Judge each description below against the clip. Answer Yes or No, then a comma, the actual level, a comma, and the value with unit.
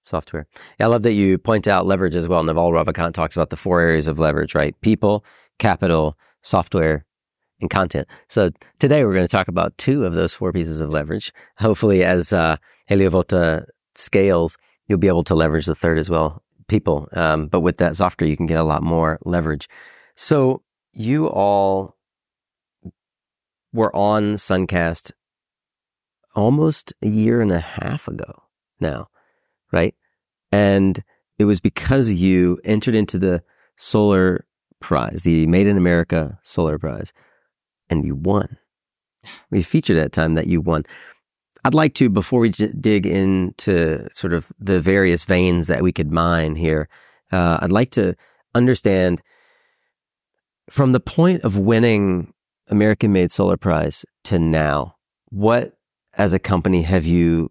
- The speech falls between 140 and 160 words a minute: Yes, average, 155 wpm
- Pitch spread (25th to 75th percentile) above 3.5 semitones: Yes, average, 4.0 semitones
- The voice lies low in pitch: Yes, very low, 90 Hz